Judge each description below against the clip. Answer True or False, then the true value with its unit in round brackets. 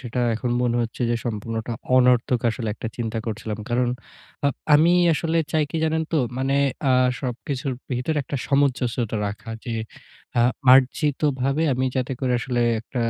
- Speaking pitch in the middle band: False (125 Hz)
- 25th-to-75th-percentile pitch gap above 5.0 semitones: False (2.8 semitones)